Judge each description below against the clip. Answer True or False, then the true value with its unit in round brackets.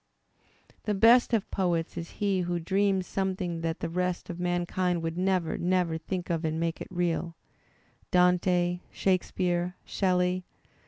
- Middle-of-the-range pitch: True (180 Hz)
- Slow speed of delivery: False (150 wpm)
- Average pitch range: False (1.5 semitones)